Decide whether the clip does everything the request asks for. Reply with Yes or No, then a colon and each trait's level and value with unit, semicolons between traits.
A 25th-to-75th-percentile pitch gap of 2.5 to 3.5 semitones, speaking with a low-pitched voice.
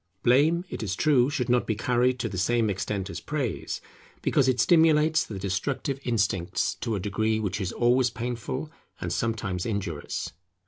No: average, 4.4 semitones; low, 120 Hz